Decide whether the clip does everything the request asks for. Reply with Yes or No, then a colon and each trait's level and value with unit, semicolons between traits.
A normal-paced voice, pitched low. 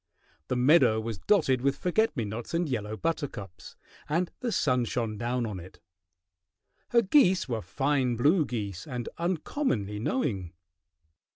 Yes: average, 145 wpm; low, 125 Hz